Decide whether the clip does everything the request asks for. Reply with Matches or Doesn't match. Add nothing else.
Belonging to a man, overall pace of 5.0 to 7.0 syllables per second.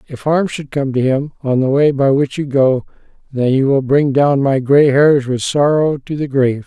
Doesn't match